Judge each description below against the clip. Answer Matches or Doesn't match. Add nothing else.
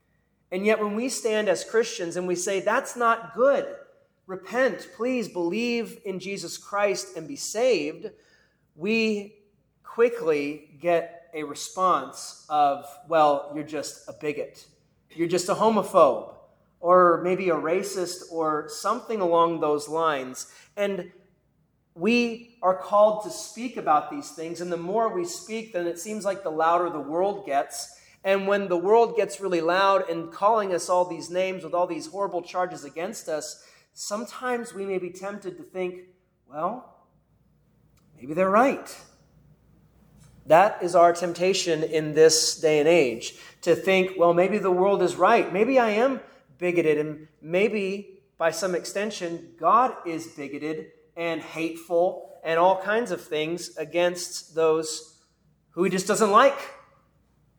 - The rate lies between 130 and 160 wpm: Matches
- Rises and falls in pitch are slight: Doesn't match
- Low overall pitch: Doesn't match